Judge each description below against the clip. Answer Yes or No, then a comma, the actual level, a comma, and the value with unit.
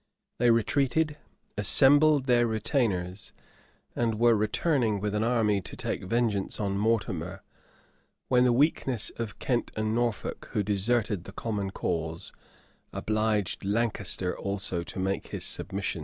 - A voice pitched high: No, low, 110 Hz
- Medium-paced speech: No, slow, 130 wpm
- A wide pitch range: No, average, 3.5 semitones